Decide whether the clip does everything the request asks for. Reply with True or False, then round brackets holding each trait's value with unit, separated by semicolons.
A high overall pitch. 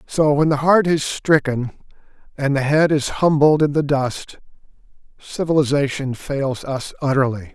False (140 Hz)